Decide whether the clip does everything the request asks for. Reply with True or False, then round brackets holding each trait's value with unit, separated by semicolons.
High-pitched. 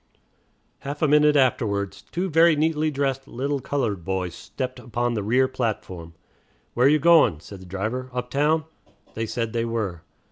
False (125 Hz)